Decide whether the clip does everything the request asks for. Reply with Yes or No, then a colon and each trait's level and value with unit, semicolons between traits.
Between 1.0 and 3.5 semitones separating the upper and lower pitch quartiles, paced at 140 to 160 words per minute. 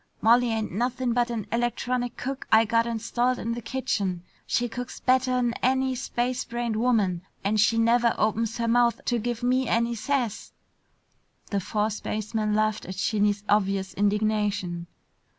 Yes: narrow, 2.4 semitones; average, 150 wpm